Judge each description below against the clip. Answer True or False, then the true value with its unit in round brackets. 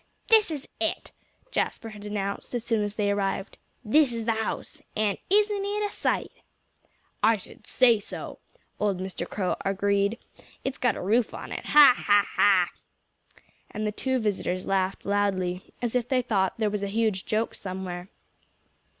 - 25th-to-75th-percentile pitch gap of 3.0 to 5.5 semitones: True (3.4 semitones)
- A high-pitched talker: True (210 Hz)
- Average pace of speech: True (165 wpm)